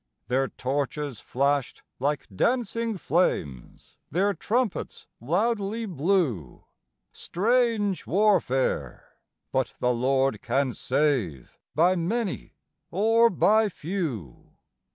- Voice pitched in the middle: Yes, medium, 170 Hz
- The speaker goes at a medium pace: No, slow, 90 wpm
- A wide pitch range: Yes, wide, 7.8 semitones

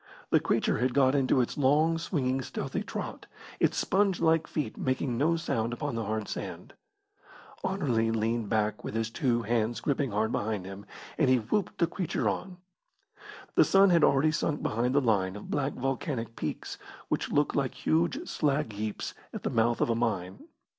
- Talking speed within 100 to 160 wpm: No, average, 180 wpm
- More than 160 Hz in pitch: No, low, 130 Hz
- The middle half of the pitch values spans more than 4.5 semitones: Yes, average, 5.1 semitones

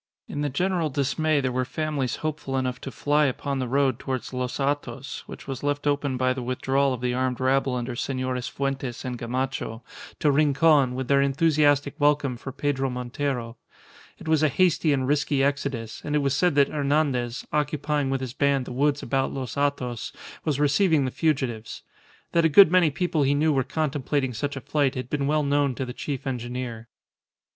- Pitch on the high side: No, medium, 140 Hz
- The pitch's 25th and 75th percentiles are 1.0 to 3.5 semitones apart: Yes, narrow, 2.4 semitones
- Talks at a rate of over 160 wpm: Yes, average, 190 wpm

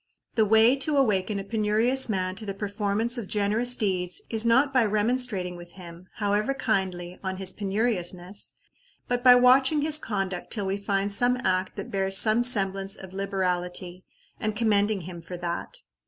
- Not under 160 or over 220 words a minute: Yes, average, 170 wpm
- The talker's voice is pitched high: Yes, high, 200 Hz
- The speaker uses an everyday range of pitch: Yes, average, 3.7 semitones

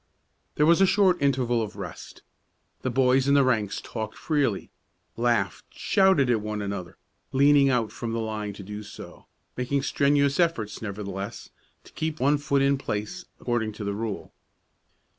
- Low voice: Yes, low, 120 Hz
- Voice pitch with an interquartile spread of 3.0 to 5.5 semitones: Yes, average, 4.8 semitones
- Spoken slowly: No, average, 160 wpm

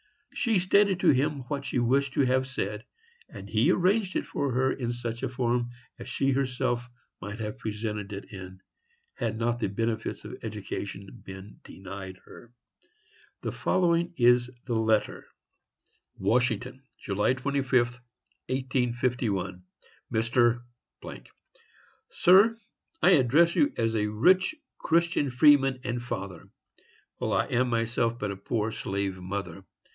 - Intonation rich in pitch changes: No, average, 4.2 semitones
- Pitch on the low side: Yes, low, 120 Hz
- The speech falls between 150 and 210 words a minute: No, slow, 135 wpm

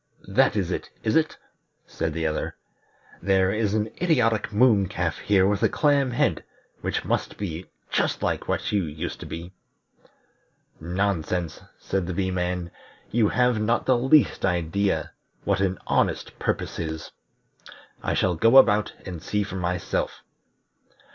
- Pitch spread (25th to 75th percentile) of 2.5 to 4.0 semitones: Yes, average, 3.7 semitones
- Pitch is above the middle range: No, very low, 95 Hz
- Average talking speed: Yes, average, 150 wpm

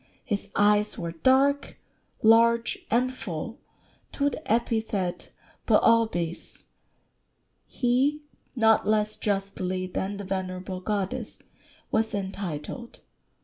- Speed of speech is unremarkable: No, slow, 100 wpm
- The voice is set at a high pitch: Yes, high, 210 Hz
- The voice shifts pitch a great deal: No, average, 3.7 semitones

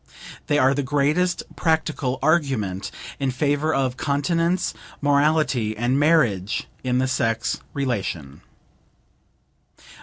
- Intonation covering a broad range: No, average, 3.9 semitones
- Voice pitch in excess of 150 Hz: No, medium, 140 Hz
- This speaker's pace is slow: Yes, slow, 100 wpm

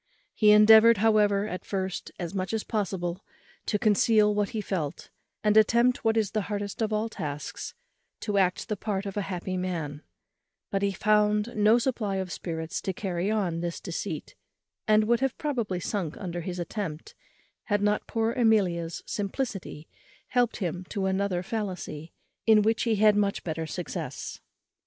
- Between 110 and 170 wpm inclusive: Yes, average, 165 wpm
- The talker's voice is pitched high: Yes, high, 205 Hz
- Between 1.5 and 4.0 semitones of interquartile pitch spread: Yes, average, 3.1 semitones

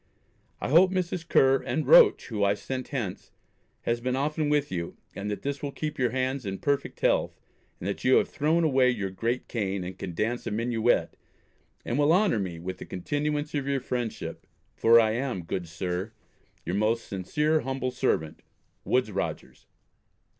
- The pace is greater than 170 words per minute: Yes, average, 180 wpm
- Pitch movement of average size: No, wide, 6.1 semitones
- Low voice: Yes, low, 125 Hz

